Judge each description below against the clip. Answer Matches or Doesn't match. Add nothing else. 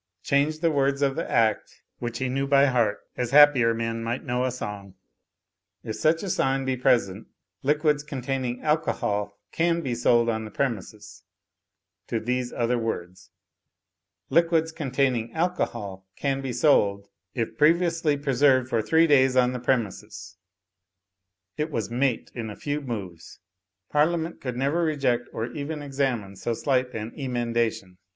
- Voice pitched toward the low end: Matches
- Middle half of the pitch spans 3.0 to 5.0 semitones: Matches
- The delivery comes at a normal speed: Matches